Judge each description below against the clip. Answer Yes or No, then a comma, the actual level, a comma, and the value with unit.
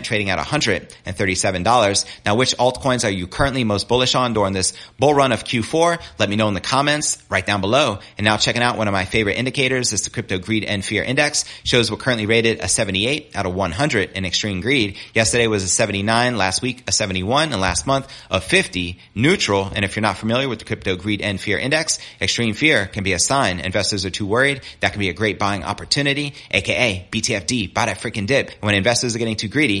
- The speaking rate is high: Yes, fast, 220 wpm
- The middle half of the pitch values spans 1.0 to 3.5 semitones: No, average, 4.0 semitones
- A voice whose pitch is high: No, low, 110 Hz